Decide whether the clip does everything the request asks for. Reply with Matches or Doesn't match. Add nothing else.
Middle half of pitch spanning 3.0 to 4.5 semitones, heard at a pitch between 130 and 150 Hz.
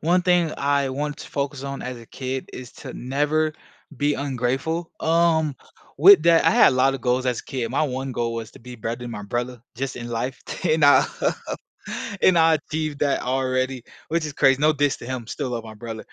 Matches